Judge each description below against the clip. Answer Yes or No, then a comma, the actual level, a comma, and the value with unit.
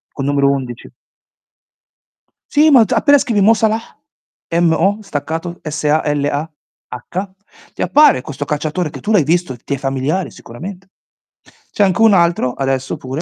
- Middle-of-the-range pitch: Yes, medium, 160 Hz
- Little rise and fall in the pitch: No, wide, 6.0 semitones